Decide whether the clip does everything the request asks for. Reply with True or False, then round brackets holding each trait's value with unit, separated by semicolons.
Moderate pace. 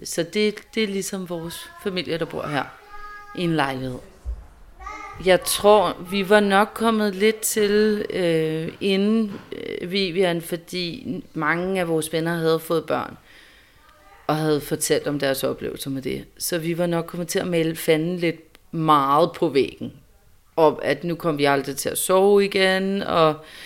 True (165 wpm)